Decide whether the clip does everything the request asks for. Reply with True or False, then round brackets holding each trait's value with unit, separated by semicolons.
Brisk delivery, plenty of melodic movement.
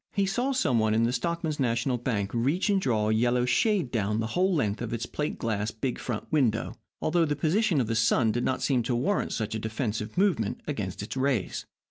True (220 wpm; 5.8 semitones)